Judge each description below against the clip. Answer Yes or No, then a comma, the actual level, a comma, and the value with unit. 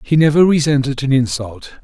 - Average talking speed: Yes, average, 165 wpm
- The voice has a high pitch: No, medium, 140 Hz